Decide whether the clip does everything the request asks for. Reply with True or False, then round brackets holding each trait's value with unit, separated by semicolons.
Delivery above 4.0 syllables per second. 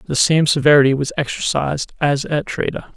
True (5.8 syllables/s)